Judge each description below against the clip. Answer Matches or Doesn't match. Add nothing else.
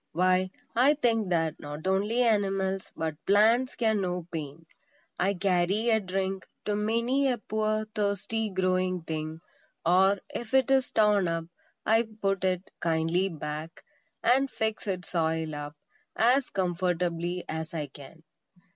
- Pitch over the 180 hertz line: Matches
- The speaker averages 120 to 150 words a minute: Matches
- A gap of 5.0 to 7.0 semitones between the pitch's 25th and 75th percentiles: Doesn't match